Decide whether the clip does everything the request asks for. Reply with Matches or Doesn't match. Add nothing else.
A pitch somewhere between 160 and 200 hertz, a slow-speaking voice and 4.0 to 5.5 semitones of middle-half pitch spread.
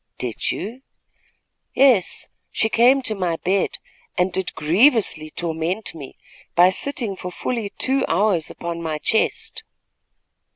Matches